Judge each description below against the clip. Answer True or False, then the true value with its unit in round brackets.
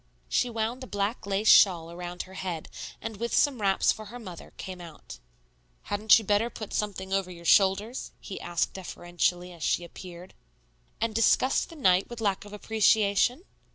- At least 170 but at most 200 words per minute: True (175 wpm)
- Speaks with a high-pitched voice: True (200 Hz)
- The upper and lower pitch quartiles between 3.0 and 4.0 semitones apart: True (3.6 semitones)